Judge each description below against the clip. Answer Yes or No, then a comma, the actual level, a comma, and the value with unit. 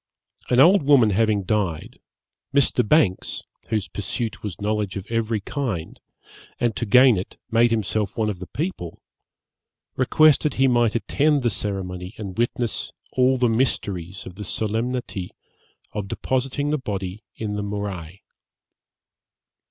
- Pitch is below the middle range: Yes, low, 110 Hz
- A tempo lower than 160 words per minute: Yes, slow, 135 wpm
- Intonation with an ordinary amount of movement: Yes, average, 4.3 semitones